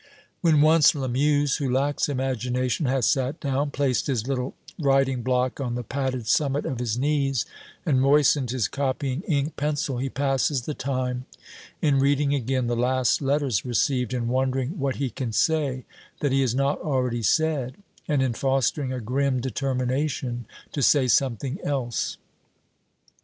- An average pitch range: No, narrow, 2.0 semitones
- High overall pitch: No, low, 135 Hz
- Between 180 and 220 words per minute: No, average, 155 wpm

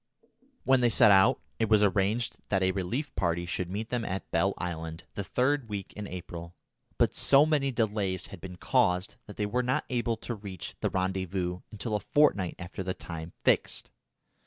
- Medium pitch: No, low, 100 Hz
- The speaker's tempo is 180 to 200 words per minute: Yes, average, 185 wpm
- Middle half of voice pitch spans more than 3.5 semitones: Yes, average, 4.2 semitones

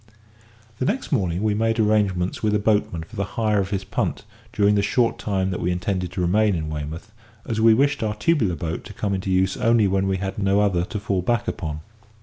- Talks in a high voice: No, low, 100 Hz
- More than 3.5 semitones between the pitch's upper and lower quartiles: No, average, 2.9 semitones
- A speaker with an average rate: No, fast, 225 wpm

